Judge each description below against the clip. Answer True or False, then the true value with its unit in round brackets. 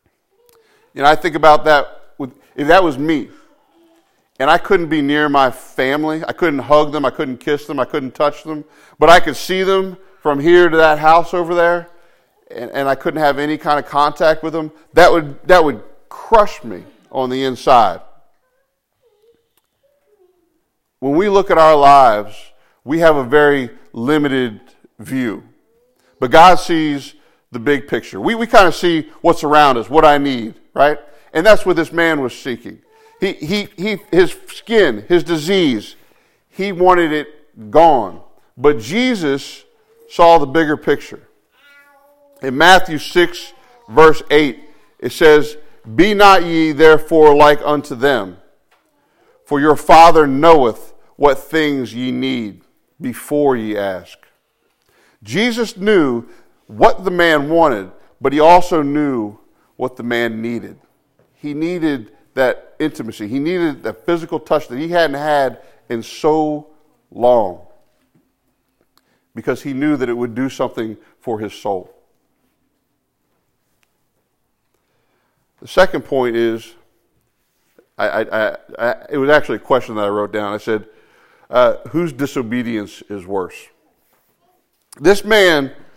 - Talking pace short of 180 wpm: True (145 wpm)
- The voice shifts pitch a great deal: False (4.4 semitones)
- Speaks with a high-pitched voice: False (155 Hz)